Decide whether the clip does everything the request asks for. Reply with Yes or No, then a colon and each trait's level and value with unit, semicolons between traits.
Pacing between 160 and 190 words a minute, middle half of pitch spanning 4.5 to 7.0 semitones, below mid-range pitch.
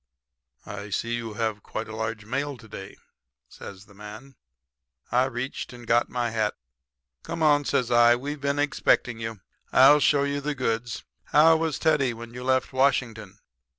No: average, 170 wpm; average, 3.9 semitones; low, 120 Hz